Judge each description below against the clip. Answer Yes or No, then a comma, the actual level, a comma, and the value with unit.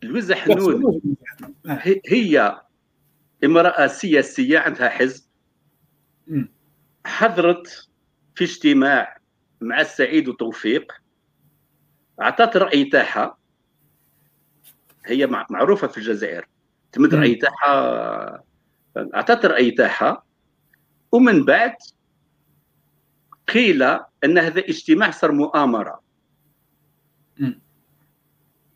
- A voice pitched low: No, high, 195 Hz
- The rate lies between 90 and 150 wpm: No, slow, 65 wpm